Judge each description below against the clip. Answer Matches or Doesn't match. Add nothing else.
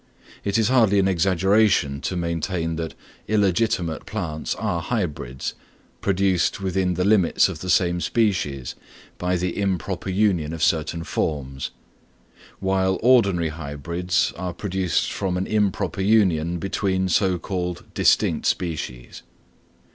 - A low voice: Matches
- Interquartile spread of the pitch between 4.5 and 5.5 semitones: Doesn't match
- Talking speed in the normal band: Doesn't match